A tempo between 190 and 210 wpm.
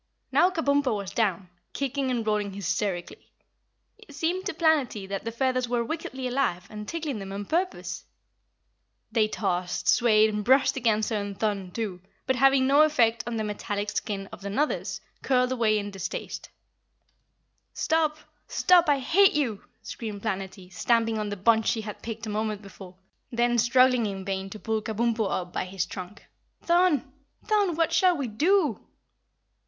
No: average, 165 wpm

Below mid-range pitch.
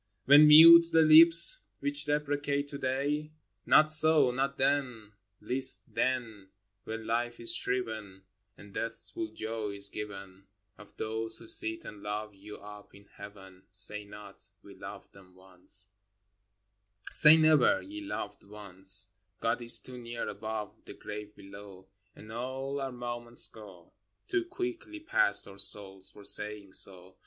Yes: low, 110 Hz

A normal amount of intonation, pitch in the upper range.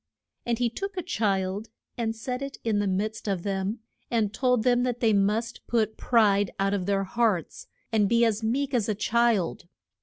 Yes: average, 3.0 semitones; high, 220 Hz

